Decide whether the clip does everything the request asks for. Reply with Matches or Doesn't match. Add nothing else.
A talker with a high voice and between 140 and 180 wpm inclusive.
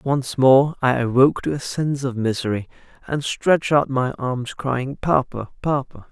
Doesn't match